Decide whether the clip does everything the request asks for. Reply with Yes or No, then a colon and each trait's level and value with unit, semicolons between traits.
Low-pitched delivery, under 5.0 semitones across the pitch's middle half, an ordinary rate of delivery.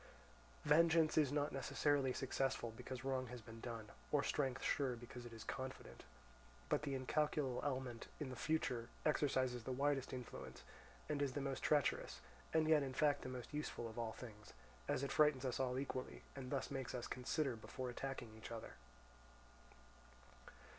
Yes: low, 130 Hz; average, 2.8 semitones; average, 165 wpm